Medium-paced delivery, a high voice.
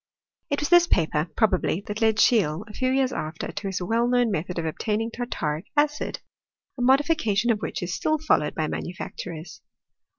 Yes: average, 175 wpm; high, 215 Hz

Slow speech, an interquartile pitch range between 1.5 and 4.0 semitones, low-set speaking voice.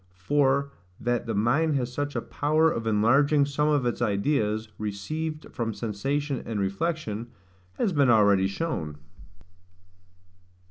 No: slow, 130 wpm; wide, 5.6 semitones; low, 125 Hz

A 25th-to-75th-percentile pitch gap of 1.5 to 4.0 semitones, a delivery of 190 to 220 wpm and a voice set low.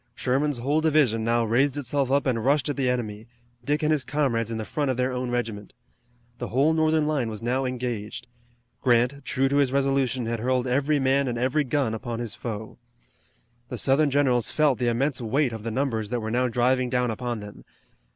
Yes: average, 3.1 semitones; fast, 205 wpm; low, 125 Hz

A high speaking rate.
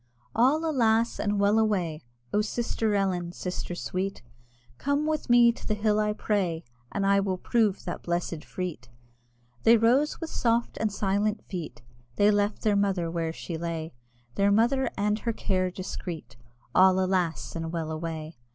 No: average, 160 wpm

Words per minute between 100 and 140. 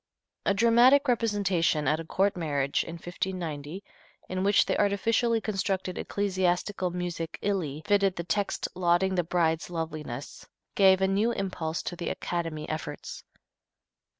Yes: slow, 135 wpm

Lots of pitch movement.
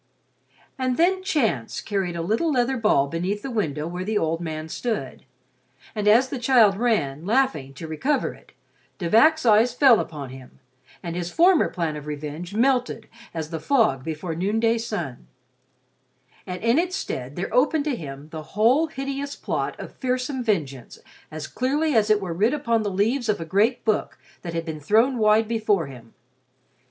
Yes: wide, 7.6 semitones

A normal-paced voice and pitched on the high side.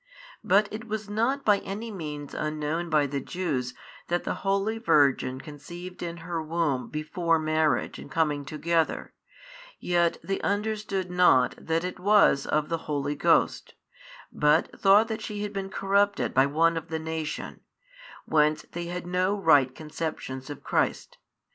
No: average, 155 wpm; medium, 165 Hz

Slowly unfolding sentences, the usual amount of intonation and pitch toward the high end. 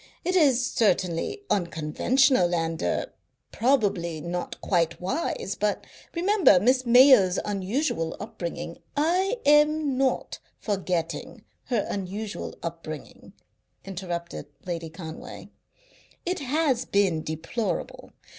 No: slow, 100 wpm; wide, 7.7 semitones; high, 200 Hz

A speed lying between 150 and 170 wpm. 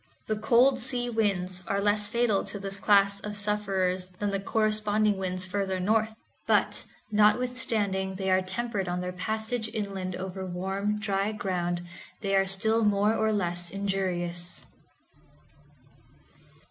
No: slow, 135 wpm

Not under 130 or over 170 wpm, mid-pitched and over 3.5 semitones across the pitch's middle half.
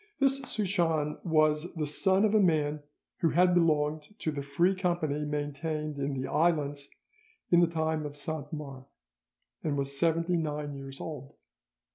No: average, 155 wpm; medium, 155 Hz; average, 2.7 semitones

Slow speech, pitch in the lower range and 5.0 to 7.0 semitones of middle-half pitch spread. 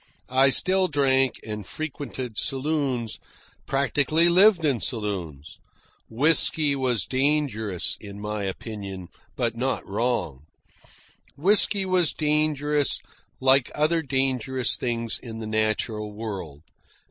Yes: slow, 105 wpm; low, 130 Hz; wide, 5.6 semitones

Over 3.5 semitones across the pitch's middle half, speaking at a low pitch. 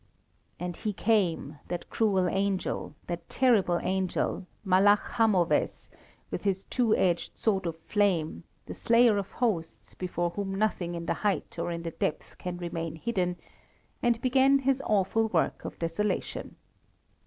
No: average, 3.9 semitones; high, 190 Hz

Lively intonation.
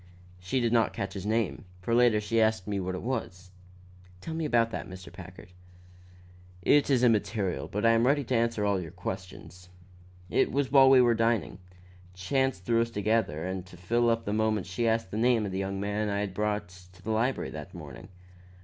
No: average, 3.9 semitones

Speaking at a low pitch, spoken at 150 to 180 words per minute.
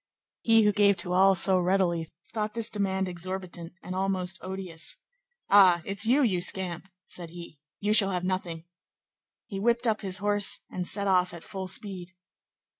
No: high, 190 Hz; average, 170 wpm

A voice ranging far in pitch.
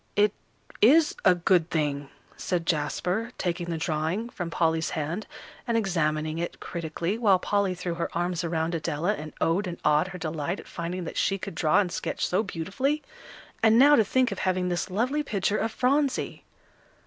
No: average, 4.2 semitones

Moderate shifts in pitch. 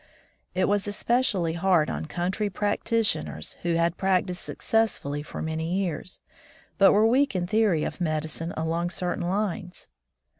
Yes: average, 3.6 semitones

